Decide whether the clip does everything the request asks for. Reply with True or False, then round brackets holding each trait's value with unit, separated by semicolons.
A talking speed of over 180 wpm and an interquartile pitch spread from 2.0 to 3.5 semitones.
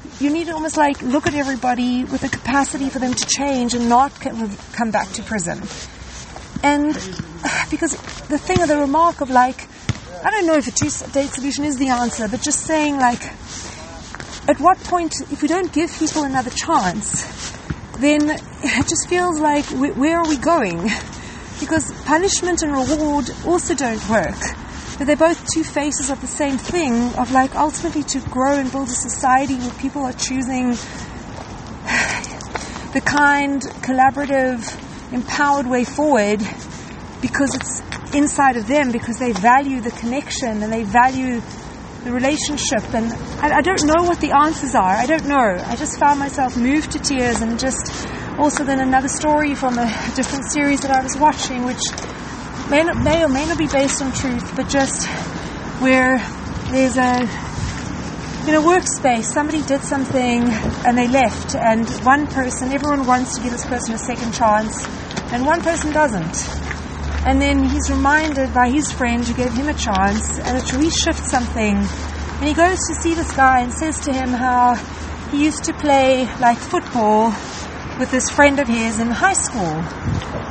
False (170 wpm; 3.1 semitones)